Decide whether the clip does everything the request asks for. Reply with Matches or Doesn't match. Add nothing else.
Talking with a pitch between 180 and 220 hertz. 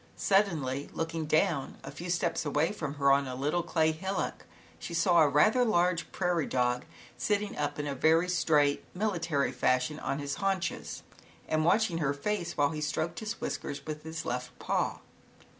Doesn't match